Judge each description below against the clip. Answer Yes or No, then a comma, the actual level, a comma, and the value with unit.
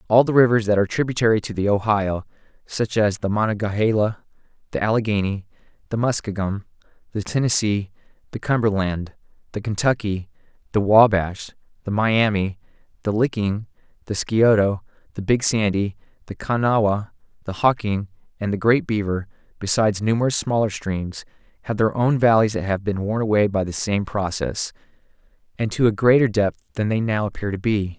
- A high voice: No, low, 105 Hz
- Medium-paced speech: Yes, average, 150 wpm